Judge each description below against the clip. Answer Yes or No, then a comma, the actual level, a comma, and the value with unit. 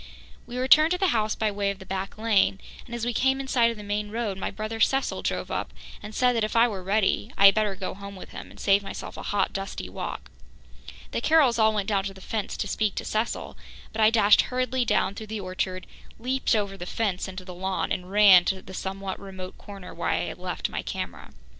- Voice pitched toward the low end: No, high, 210 Hz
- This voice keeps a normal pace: No, fast, 240 wpm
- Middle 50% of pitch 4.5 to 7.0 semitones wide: No, average, 2.8 semitones